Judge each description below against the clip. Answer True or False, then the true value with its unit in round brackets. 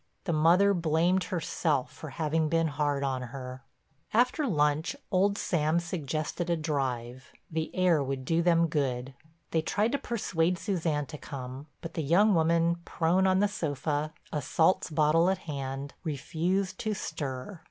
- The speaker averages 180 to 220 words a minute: False (155 wpm)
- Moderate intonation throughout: True (3.6 semitones)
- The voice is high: False (160 Hz)